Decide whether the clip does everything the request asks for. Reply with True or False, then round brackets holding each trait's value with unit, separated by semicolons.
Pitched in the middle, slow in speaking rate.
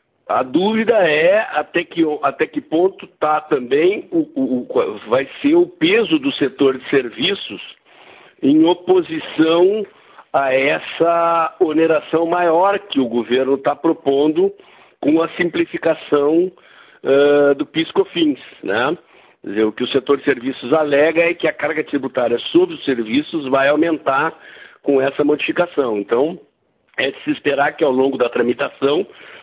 False (165 Hz; 145 wpm)